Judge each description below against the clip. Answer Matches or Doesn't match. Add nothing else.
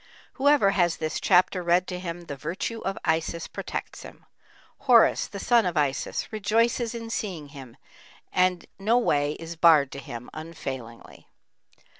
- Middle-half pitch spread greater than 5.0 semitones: Matches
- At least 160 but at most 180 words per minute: Doesn't match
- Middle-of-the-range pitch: Matches